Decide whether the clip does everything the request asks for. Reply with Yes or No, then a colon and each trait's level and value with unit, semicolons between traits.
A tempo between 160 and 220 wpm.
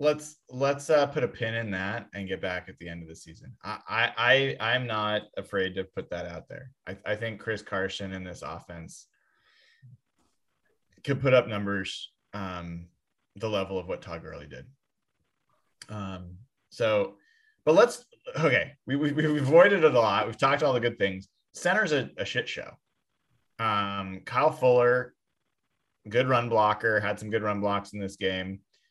Yes: average, 175 wpm